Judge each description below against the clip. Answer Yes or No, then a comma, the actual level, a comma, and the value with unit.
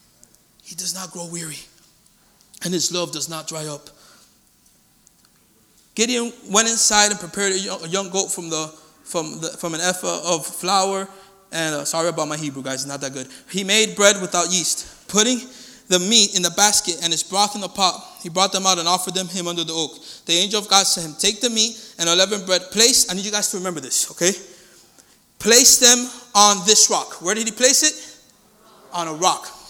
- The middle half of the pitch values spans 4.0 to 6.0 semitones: No, average, 3.5 semitones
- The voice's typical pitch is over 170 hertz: Yes, medium, 185 Hz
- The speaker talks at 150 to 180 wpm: No, fast, 205 wpm